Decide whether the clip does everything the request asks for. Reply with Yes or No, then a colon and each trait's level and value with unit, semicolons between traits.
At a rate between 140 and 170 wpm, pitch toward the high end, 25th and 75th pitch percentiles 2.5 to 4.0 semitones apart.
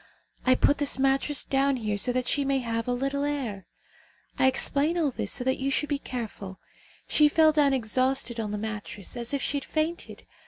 No: fast, 205 wpm; very high, 265 Hz; average, 3.4 semitones